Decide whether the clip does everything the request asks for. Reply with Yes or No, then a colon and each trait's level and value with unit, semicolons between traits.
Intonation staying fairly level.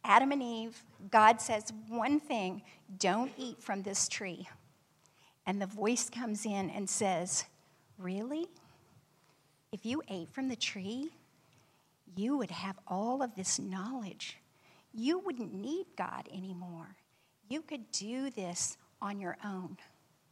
No: average, 4.6 semitones